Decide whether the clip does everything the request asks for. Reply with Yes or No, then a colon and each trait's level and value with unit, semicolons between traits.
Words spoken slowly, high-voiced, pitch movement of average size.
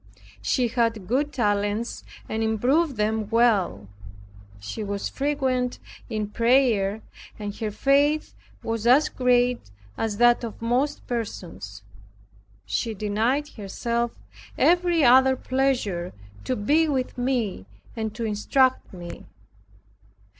Yes: slow, 110 wpm; high, 235 Hz; average, 3.9 semitones